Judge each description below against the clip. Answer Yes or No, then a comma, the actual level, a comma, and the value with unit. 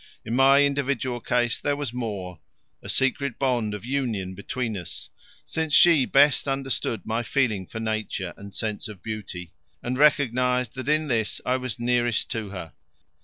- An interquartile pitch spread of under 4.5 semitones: Yes, average, 4.0 semitones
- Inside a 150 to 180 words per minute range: Yes, average, 165 wpm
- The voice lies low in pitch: Yes, low, 120 Hz